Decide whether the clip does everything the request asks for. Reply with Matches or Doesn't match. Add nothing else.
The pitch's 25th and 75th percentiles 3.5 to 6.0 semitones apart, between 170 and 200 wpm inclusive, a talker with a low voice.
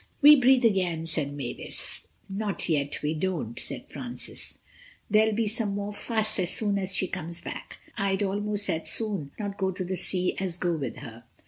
Doesn't match